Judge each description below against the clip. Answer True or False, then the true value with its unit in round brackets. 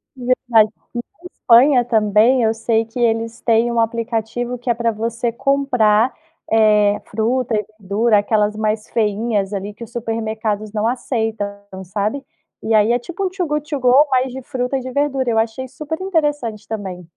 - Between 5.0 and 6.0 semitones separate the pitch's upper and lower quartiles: False (2.8 semitones)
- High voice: True (230 Hz)